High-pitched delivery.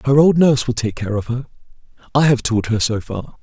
No: low, 125 Hz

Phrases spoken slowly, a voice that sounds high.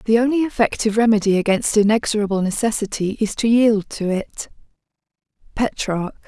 Yes: slow, 125 wpm; high, 215 Hz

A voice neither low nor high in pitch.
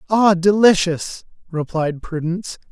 Yes: medium, 180 Hz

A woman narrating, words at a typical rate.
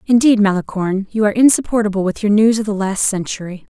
Yes: female; average, 190 wpm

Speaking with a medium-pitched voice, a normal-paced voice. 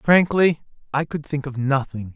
Yes: medium, 145 Hz; average, 165 wpm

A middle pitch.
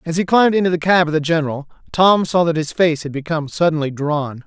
Yes: medium, 160 Hz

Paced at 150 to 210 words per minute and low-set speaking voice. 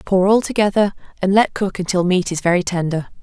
No: fast, 205 wpm; high, 190 Hz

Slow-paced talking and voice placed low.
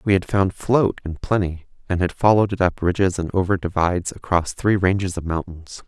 No: fast, 205 wpm; very low, 90 Hz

